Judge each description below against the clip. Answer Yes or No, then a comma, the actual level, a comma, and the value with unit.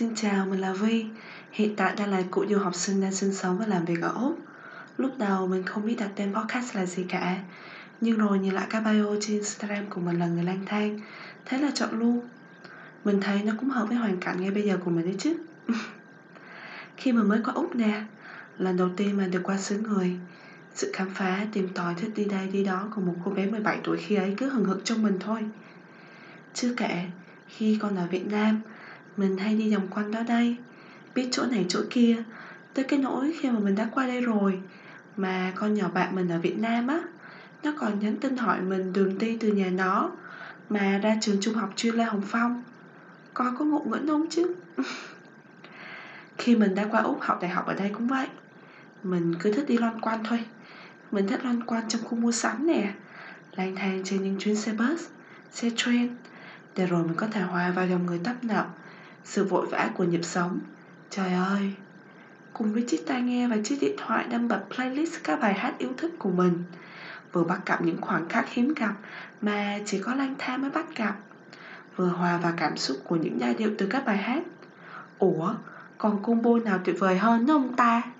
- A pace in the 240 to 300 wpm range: No, average, 215 wpm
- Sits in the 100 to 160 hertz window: No, high, 210 Hz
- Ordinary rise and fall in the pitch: Yes, average, 3.7 semitones